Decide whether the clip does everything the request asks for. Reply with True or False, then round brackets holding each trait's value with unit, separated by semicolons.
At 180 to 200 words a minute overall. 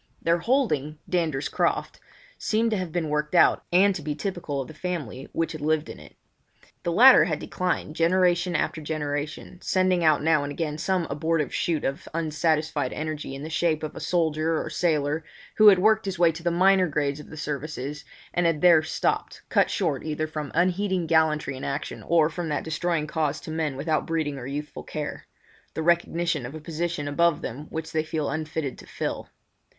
True (190 wpm)